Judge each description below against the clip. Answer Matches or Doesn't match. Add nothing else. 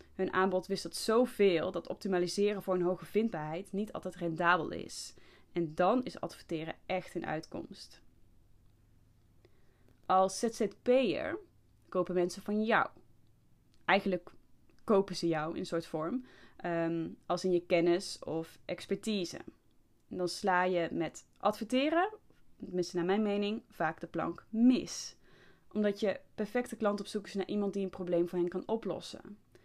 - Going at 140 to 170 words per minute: Matches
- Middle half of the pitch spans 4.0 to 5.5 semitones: Doesn't match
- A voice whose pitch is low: Doesn't match